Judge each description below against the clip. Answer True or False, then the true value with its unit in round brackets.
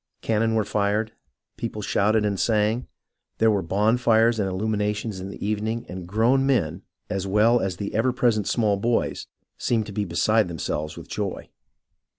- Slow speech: False (165 wpm)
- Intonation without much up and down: True (2.1 semitones)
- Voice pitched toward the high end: False (105 Hz)